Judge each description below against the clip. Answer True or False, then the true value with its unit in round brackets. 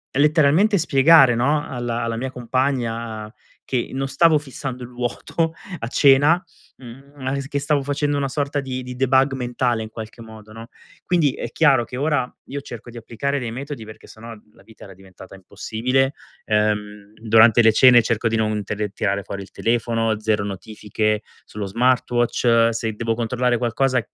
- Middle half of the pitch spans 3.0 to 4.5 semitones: True (3.5 semitones)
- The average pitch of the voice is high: False (120 Hz)